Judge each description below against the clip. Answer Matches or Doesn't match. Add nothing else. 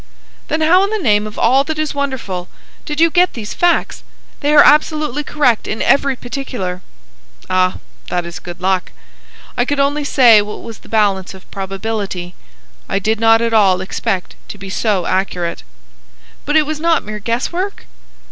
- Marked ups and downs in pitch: Matches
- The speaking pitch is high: Matches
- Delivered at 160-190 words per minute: Matches